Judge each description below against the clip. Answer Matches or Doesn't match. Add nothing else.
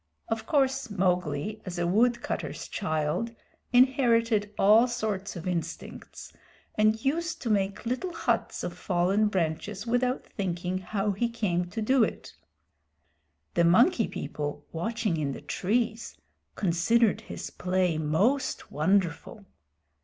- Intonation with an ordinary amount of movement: Matches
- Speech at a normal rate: Doesn't match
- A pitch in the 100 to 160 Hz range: Doesn't match